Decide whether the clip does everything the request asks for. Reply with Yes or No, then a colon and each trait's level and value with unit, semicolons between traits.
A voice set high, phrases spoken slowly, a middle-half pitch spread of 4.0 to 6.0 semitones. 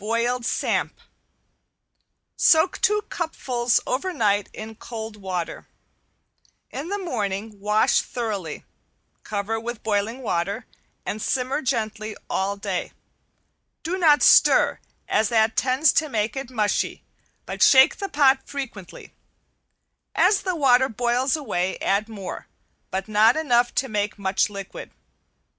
Yes: high, 225 Hz; slow, 125 wpm; average, 4.4 semitones